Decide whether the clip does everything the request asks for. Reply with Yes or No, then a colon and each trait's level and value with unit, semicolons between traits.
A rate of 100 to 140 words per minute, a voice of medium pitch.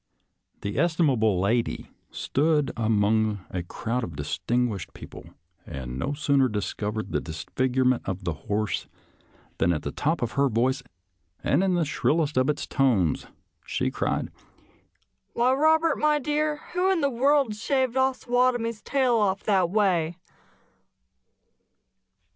Yes: slow, 135 wpm; medium, 145 Hz